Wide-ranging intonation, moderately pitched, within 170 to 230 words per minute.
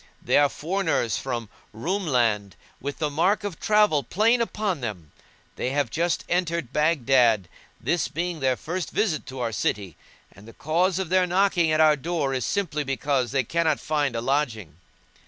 Yes: wide, 5.9 semitones; medium, 150 Hz; average, 175 wpm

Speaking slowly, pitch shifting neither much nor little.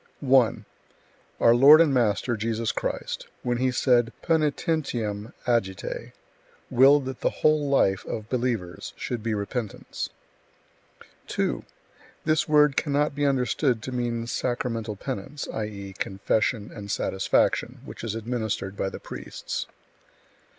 Yes: slow, 120 wpm; average, 4.1 semitones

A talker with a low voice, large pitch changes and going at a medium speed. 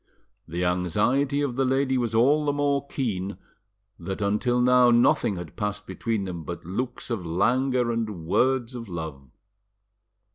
Yes: low, 115 Hz; wide, 6.0 semitones; average, 150 wpm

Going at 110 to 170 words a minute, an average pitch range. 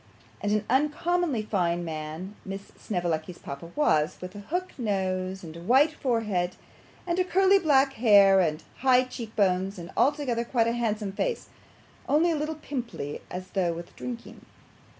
No: average, 155 wpm; wide, 6.8 semitones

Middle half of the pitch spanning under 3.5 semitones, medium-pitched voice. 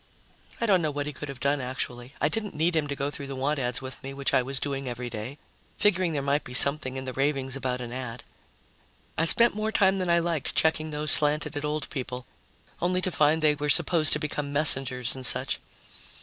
Yes: average, 3.1 semitones; medium, 145 Hz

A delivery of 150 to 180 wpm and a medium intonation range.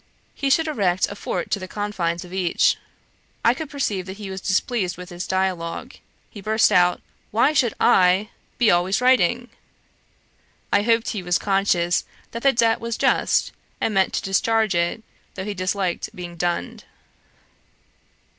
Yes: average, 160 wpm; average, 4.0 semitones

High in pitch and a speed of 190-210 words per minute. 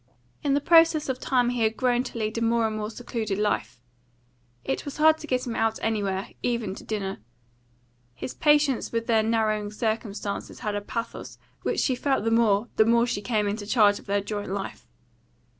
Yes: high, 225 Hz; average, 195 wpm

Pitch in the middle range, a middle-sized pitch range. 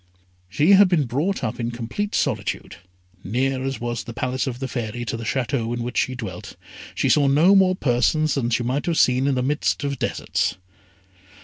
No: low, 130 Hz; average, 3.4 semitones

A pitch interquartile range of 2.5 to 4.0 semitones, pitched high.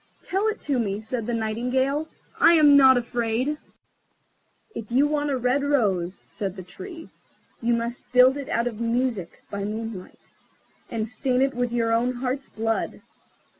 Yes: average, 3.3 semitones; high, 245 Hz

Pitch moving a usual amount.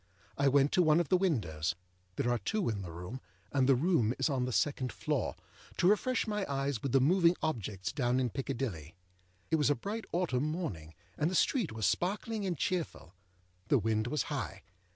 No: wide, 7.5 semitones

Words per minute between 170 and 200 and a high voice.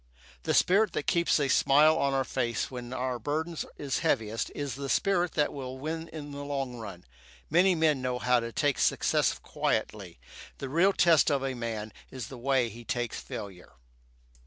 No: average, 180 wpm; low, 135 Hz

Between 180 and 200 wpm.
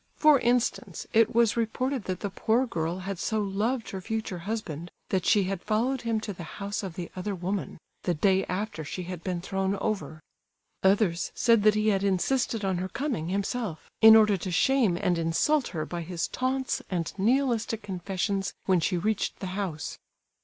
Yes: average, 185 wpm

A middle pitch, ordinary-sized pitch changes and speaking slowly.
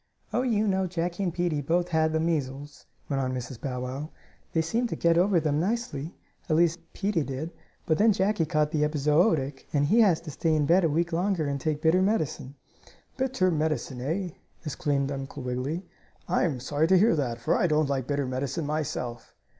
No: medium, 155 Hz; average, 4.0 semitones; average, 200 wpm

